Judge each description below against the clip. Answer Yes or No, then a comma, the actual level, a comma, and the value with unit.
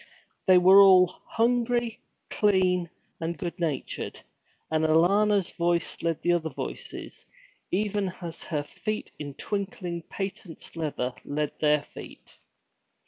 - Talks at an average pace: No, slow, 120 wpm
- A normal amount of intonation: Yes, average, 3.7 semitones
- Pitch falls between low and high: Yes, medium, 180 Hz